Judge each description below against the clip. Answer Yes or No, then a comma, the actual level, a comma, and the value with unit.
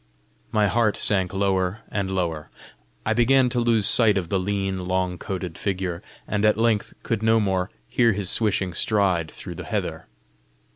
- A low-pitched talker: Yes, low, 100 Hz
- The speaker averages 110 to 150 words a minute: No, average, 165 wpm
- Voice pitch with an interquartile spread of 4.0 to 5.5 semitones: No, average, 3.0 semitones